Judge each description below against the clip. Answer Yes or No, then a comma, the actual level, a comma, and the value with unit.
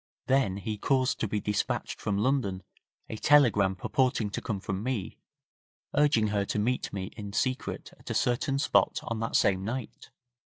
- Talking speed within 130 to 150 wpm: No, average, 170 wpm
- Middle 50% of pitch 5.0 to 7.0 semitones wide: No, average, 4.4 semitones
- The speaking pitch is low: Yes, low, 110 Hz